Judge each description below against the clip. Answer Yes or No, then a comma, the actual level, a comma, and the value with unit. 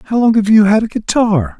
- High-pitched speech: Yes, high, 205 Hz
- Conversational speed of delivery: No, fast, 265 wpm